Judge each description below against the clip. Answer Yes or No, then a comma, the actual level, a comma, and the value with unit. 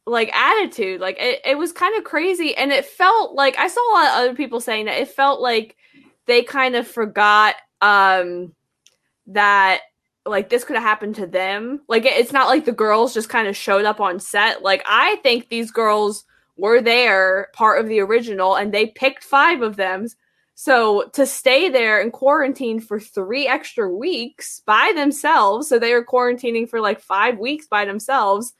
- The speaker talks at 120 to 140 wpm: No, average, 190 wpm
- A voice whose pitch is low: No, high, 230 Hz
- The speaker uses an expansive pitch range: No, average, 4.7 semitones